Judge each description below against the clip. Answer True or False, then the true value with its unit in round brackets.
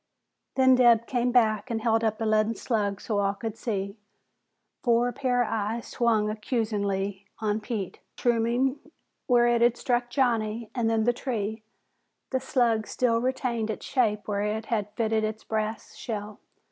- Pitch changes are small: True (2.2 semitones)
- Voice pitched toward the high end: True (225 Hz)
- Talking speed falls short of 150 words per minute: False (160 wpm)